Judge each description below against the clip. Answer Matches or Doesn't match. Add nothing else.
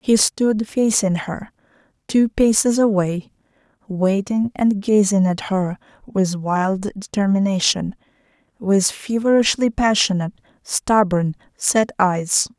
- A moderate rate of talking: Doesn't match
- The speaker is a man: Doesn't match